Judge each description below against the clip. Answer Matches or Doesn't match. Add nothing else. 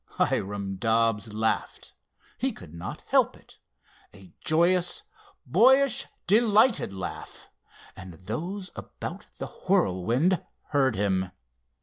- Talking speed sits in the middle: Doesn't match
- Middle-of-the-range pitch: Doesn't match